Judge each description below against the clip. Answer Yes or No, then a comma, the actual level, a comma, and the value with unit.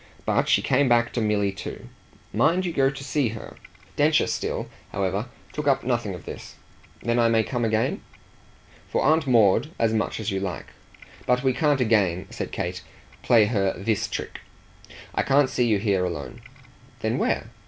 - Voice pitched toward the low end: Yes, low, 115 Hz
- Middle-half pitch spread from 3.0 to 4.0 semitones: No, average, 4.8 semitones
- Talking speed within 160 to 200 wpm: Yes, average, 175 wpm